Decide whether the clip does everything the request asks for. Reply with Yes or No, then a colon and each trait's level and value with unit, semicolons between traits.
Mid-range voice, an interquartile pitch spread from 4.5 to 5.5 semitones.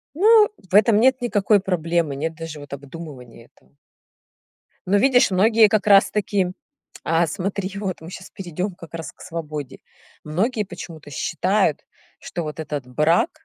Yes: medium, 175 Hz; average, 4.9 semitones